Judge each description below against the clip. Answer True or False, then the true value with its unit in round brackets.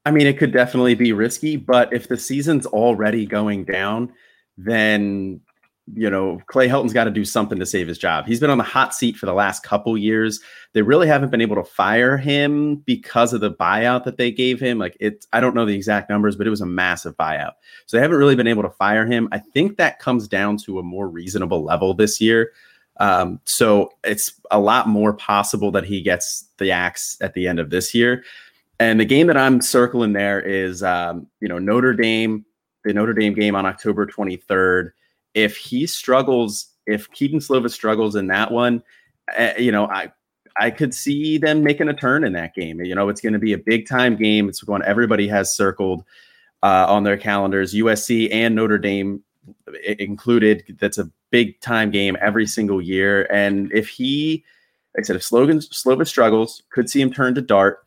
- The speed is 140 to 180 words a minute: False (205 wpm)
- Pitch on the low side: True (110 Hz)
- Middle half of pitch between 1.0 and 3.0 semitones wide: False (3.6 semitones)